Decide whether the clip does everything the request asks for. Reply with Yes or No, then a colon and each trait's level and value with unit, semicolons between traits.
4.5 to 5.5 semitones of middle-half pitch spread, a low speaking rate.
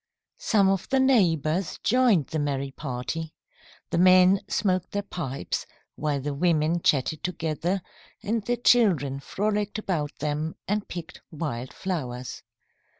Yes: average, 5.2 semitones; slow, 130 wpm